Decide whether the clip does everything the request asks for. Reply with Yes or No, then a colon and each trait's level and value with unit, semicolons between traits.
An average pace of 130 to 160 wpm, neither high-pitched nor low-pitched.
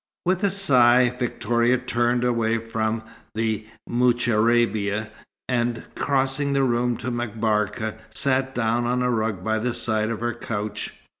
No: average, 140 wpm; low, 120 Hz